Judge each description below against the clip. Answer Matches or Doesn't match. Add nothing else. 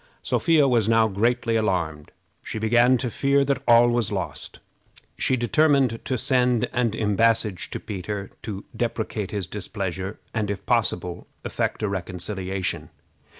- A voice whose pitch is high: Doesn't match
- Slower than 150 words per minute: Matches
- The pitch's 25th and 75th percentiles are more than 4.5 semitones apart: Doesn't match